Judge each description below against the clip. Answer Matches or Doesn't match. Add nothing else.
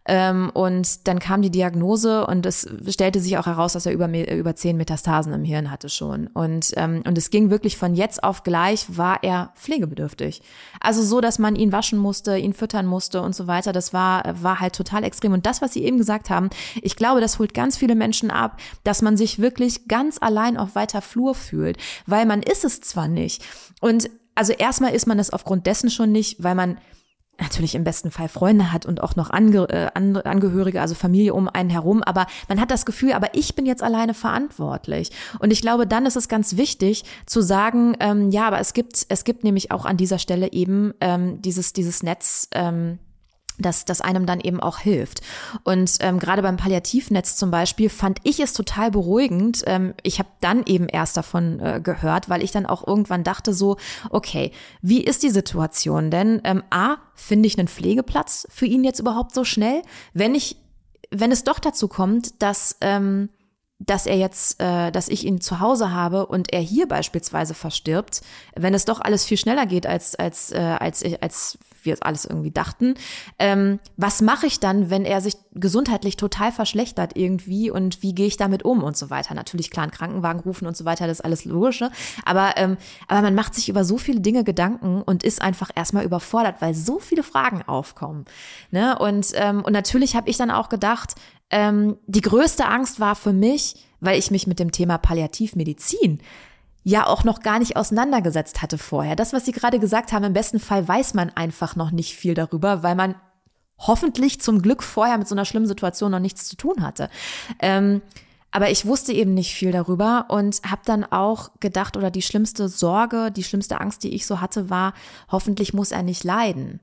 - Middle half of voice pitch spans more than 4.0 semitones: Doesn't match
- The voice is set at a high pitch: Matches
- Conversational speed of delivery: Doesn't match